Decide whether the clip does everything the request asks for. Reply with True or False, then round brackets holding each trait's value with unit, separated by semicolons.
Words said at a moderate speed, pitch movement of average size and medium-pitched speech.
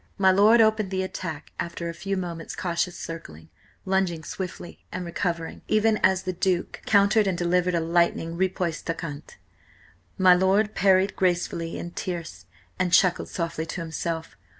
False (155 wpm; 2.2 semitones; 180 Hz)